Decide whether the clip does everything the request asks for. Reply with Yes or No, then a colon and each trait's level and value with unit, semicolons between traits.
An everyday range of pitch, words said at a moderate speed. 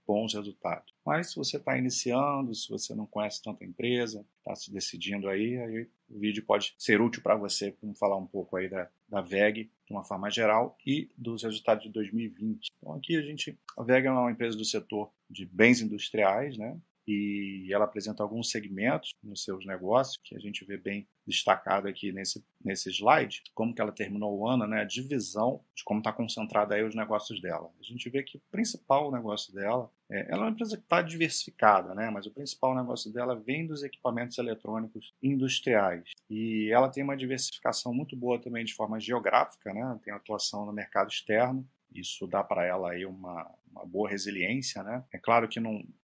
No: average, 3.6 semitones; fast, 195 wpm